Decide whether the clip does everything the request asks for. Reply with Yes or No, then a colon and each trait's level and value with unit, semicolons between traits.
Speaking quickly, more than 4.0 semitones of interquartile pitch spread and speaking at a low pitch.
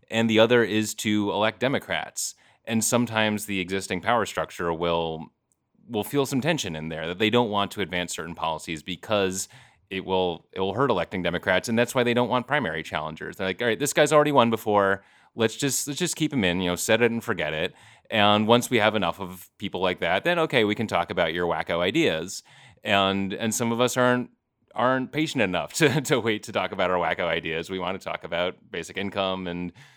Yes: fast, 220 wpm; average, 4.6 semitones; low, 105 Hz